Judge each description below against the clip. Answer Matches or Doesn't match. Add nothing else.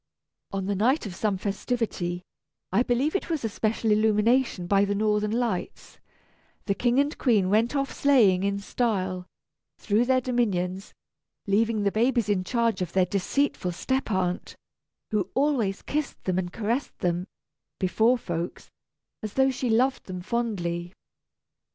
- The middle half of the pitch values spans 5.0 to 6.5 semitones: Doesn't match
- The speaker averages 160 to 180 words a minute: Doesn't match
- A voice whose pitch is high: Matches